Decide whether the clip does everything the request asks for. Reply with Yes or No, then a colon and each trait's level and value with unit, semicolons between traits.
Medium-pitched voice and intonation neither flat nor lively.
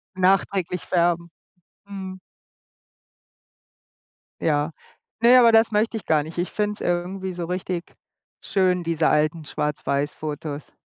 Yes: medium, 180 Hz; average, 3.4 semitones